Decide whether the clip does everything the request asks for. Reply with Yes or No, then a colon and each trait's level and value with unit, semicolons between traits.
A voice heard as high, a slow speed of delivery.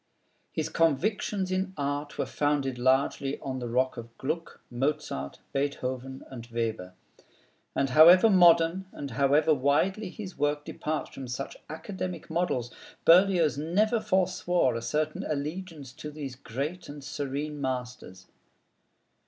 No: medium, 145 Hz; slow, 130 wpm